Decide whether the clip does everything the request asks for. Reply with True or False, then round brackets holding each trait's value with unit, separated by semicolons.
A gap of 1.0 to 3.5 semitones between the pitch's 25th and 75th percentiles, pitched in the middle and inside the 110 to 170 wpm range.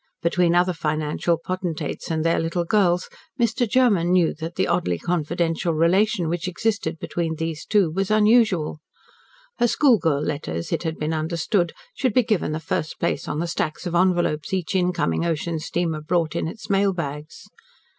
True (3.0 semitones; 170 Hz; 165 wpm)